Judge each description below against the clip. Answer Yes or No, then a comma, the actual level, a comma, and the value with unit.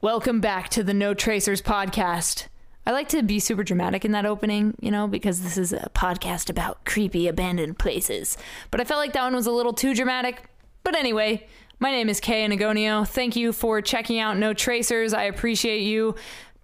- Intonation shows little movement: Yes, narrow, 2.3 semitones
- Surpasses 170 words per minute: Yes, average, 200 wpm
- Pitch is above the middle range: Yes, high, 215 Hz